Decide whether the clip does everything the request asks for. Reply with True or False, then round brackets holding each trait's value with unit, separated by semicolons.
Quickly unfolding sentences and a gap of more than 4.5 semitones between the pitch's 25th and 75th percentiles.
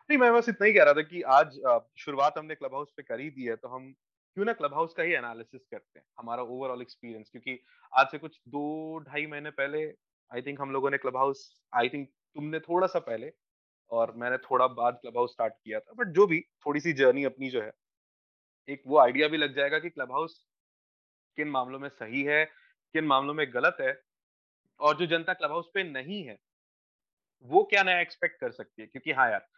True (220 wpm; 5.2 semitones)